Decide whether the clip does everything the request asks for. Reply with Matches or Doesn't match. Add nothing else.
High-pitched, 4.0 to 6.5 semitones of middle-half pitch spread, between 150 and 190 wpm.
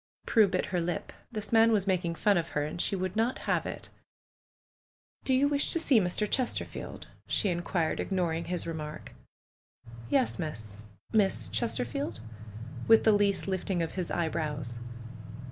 Doesn't match